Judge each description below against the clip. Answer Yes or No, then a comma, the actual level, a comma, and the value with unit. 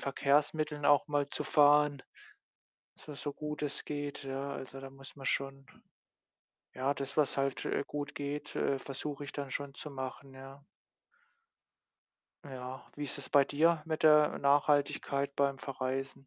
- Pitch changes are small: Yes, narrow, 1.3 semitones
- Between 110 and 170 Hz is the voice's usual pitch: Yes, medium, 140 Hz